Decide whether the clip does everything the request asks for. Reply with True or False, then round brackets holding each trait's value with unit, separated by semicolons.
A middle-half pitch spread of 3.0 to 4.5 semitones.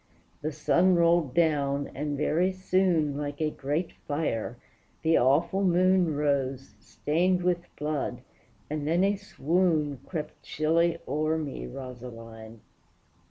True (3.5 semitones)